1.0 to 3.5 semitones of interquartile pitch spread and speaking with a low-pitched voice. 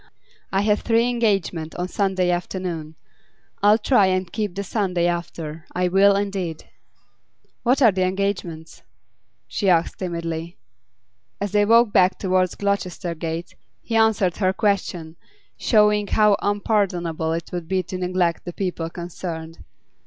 No: average, 3.0 semitones; medium, 185 Hz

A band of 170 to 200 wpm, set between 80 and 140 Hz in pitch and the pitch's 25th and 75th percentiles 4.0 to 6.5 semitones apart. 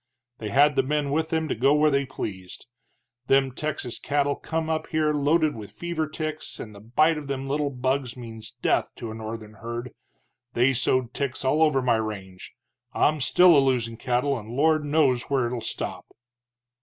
Yes: average, 190 wpm; low, 135 Hz; average, 4.3 semitones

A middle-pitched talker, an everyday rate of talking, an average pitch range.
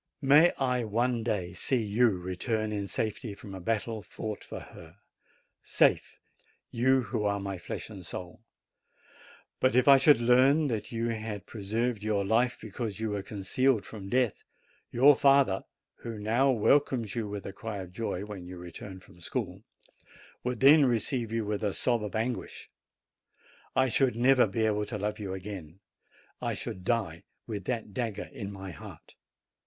No: low, 110 Hz; average, 170 wpm; average, 3.6 semitones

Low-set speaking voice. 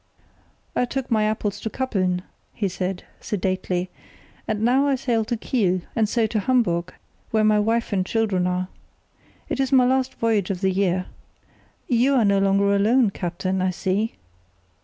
No: high, 210 Hz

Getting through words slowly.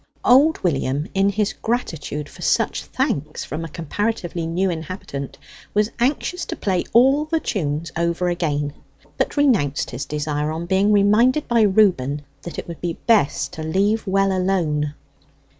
No: average, 155 wpm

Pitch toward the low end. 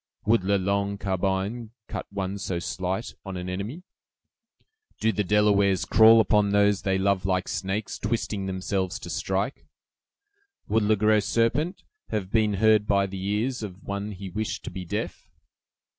Yes: low, 100 Hz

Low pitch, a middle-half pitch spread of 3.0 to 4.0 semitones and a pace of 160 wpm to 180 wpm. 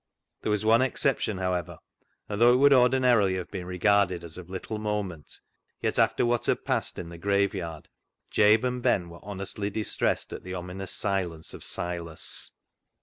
Yes: low, 100 Hz; average, 3.4 semitones; average, 175 wpm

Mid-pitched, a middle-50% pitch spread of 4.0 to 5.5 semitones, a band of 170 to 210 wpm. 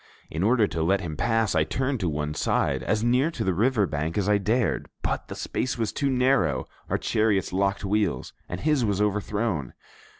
No: low, 105 Hz; average, 5.1 semitones; average, 200 wpm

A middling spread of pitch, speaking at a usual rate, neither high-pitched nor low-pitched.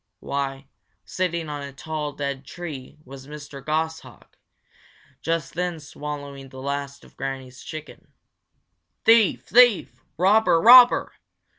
No: average, 3.5 semitones; slow, 115 wpm; medium, 150 Hz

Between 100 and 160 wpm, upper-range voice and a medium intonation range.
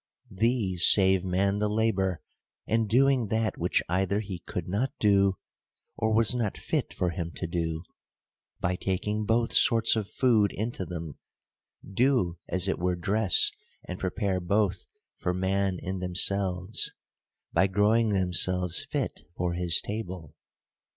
No: average, 140 wpm; very low, 95 Hz; average, 3.1 semitones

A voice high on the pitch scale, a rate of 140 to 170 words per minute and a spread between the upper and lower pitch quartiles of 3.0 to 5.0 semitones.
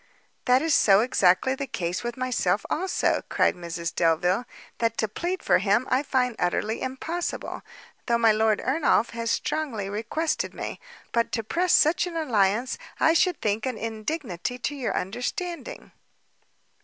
No: high, 235 Hz; average, 155 wpm; wide, 5.4 semitones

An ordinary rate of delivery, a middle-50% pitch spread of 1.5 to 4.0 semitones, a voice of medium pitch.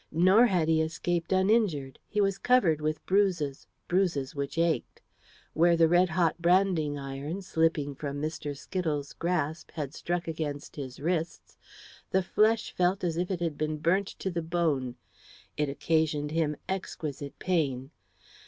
Yes: average, 150 wpm; average, 3.5 semitones; medium, 165 Hz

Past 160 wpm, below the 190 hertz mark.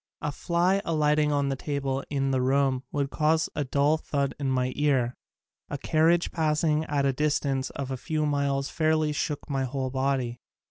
Yes: average, 180 wpm; medium, 140 Hz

